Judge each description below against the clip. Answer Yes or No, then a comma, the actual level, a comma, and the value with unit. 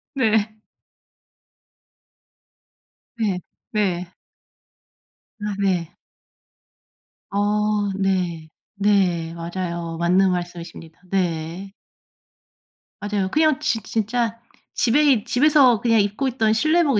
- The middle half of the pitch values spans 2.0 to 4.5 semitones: Yes, average, 4.1 semitones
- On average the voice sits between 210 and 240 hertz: No, high, 200 Hz